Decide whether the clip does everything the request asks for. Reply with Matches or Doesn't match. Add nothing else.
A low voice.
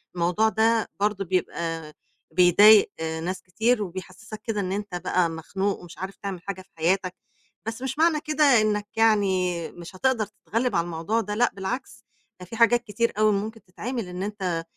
Doesn't match